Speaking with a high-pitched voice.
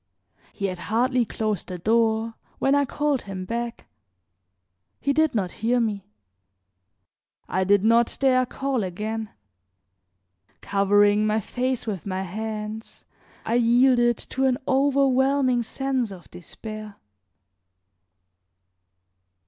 Yes: high, 225 Hz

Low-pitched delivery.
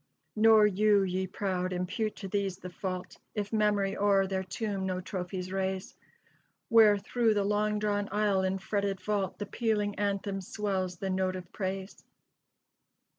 No: high, 195 Hz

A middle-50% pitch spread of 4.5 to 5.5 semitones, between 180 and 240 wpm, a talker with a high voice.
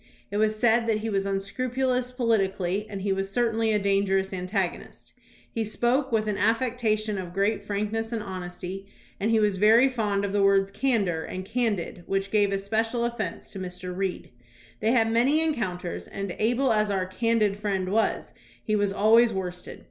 No: average, 2.8 semitones; average, 185 wpm; high, 210 Hz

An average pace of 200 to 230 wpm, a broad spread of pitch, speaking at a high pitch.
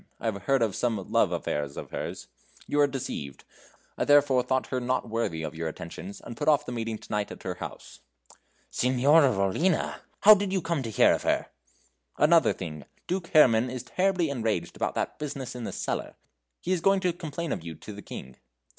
No: fast, 205 wpm; wide, 6.8 semitones; low, 125 Hz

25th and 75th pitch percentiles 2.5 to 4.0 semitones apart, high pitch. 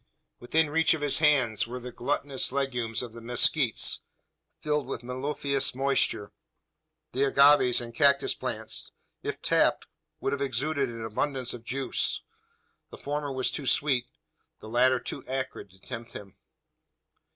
No: average, 2.8 semitones; low, 130 Hz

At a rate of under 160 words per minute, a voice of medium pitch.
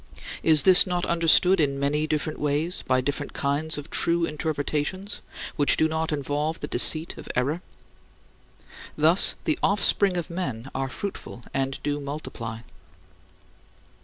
Yes: average, 140 wpm; medium, 155 Hz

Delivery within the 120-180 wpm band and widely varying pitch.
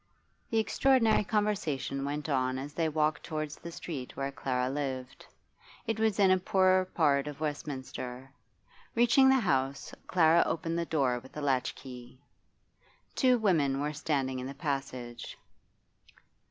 Yes: average, 140 wpm; wide, 5.7 semitones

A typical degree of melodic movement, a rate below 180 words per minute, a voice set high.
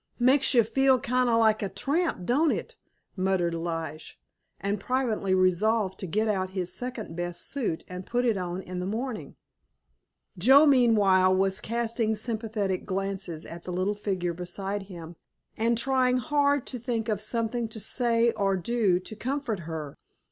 Yes: average, 4.5 semitones; average, 160 wpm; high, 210 Hz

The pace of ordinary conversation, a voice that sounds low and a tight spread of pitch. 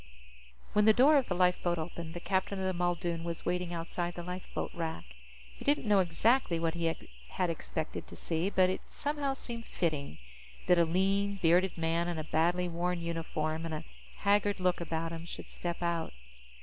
No: average, 190 wpm; medium, 175 Hz; narrow, 2.3 semitones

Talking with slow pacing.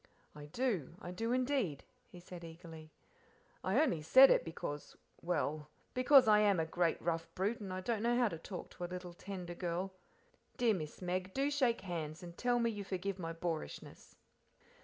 No: average, 180 wpm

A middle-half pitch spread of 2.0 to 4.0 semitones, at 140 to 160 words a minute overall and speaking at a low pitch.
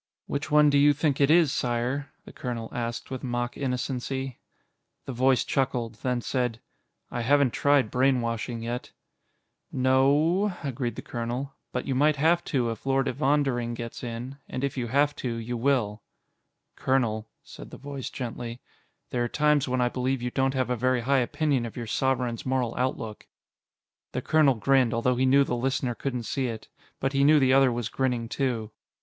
No: narrow, 2.4 semitones; average, 185 wpm; low, 130 Hz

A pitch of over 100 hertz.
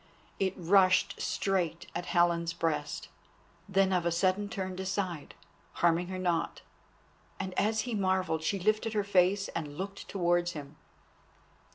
Yes: medium, 185 Hz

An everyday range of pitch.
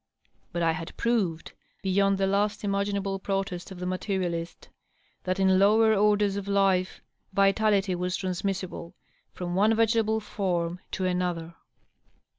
No: narrow, 1.9 semitones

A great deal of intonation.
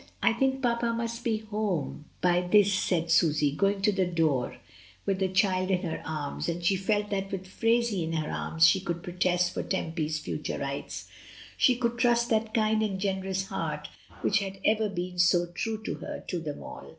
No: average, 3.9 semitones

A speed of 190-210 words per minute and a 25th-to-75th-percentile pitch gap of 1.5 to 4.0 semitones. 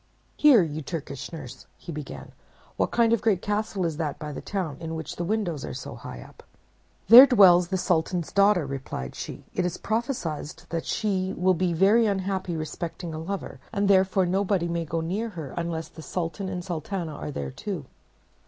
Yes: average, 195 wpm; average, 3.7 semitones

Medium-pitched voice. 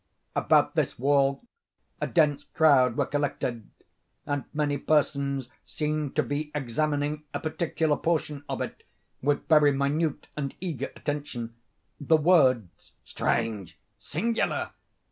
Yes: medium, 145 Hz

